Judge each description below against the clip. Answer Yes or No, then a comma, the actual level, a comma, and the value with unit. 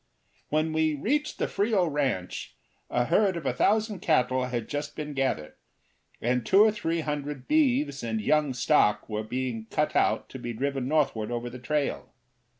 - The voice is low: No, medium, 145 Hz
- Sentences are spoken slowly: No, average, 170 wpm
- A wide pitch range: No, average, 4.9 semitones